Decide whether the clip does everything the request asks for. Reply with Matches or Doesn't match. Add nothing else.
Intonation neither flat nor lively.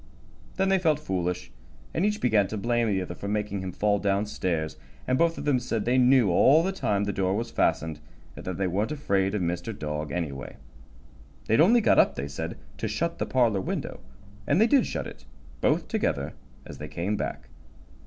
Doesn't match